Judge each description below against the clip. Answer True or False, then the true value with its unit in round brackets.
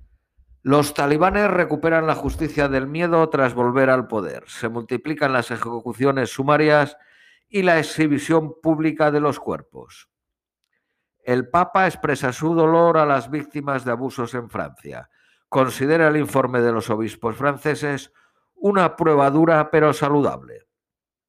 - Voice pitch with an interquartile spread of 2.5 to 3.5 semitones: False (4.0 semitones)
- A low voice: False (145 Hz)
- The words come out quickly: False (135 wpm)